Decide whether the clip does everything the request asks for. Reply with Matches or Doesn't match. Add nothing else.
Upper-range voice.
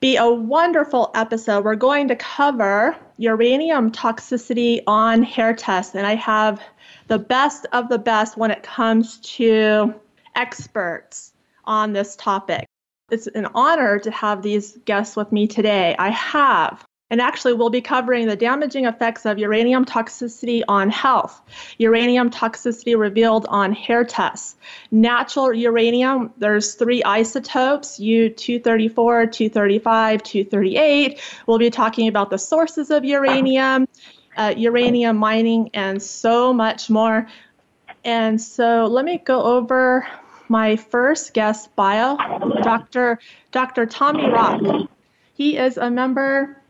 Matches